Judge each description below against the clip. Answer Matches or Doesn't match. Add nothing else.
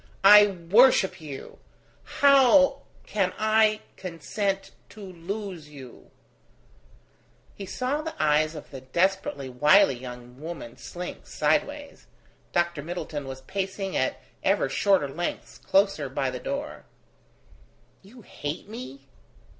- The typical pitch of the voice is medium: Matches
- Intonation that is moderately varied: Doesn't match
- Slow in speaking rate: Matches